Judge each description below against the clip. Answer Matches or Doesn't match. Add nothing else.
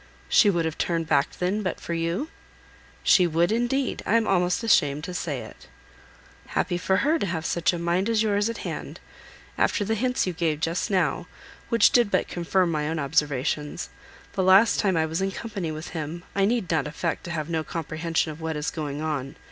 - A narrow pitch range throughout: Doesn't match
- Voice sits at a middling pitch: Matches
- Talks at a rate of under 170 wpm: Doesn't match